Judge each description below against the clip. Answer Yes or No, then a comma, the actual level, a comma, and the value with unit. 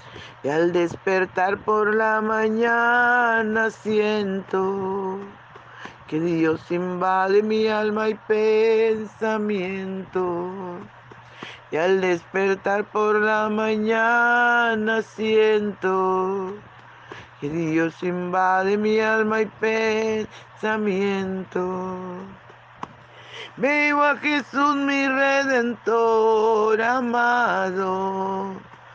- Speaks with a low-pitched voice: No, high, 210 Hz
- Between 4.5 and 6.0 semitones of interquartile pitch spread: No, average, 2.8 semitones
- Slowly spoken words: Yes, slow, 70 wpm